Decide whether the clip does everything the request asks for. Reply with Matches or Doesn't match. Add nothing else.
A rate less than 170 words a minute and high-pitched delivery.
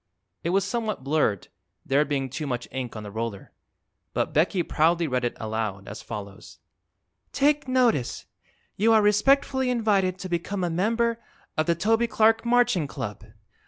Doesn't match